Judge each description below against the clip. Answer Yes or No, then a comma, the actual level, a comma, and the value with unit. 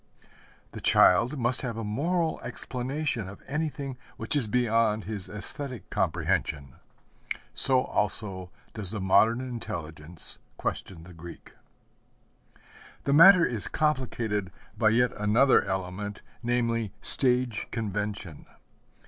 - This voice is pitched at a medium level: No, low, 115 Hz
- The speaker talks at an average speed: No, slow, 110 wpm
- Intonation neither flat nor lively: Yes, average, 4.3 semitones